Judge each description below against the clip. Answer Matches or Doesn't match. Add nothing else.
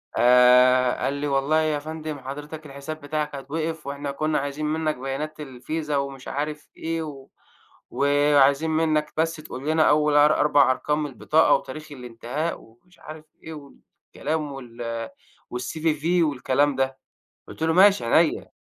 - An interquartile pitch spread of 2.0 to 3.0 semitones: Matches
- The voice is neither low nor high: Matches